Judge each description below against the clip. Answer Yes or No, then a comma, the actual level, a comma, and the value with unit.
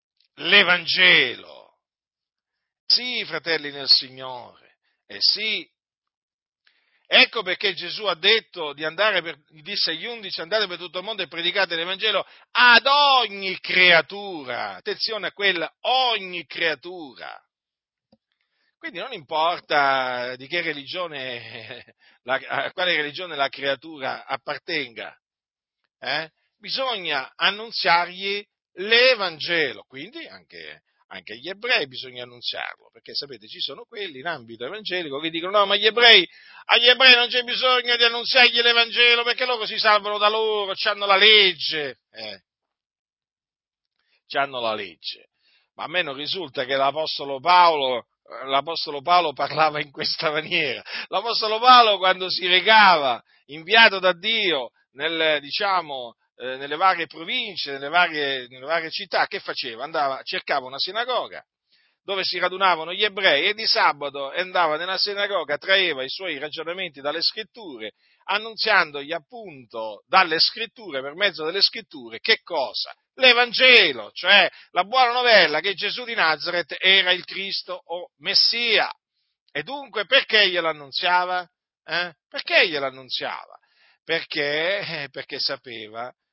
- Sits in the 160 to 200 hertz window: Yes, medium, 185 Hz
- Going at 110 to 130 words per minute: Yes, average, 125 wpm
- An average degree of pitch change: No, wide, 6.1 semitones